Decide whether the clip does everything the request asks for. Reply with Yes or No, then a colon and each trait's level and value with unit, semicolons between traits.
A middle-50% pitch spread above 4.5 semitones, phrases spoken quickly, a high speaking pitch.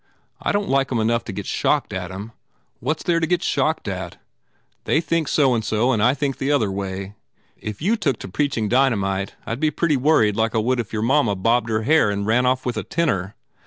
No: wide, 5.5 semitones; fast, 240 wpm; low, 120 Hz